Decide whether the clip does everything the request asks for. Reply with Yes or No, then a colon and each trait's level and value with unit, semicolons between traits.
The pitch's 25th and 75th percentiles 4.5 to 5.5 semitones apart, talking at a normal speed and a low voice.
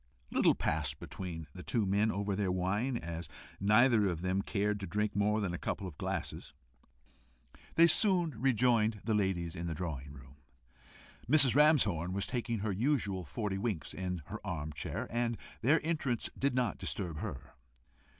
Yes: average, 5.2 semitones; average, 170 wpm; low, 100 Hz